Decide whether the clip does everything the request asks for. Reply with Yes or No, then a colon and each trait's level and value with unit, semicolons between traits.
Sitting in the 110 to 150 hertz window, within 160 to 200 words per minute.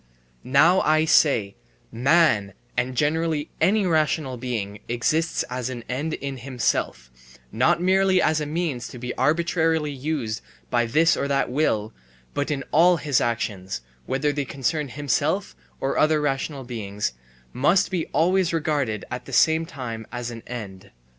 No: medium, 140 Hz; average, 150 wpm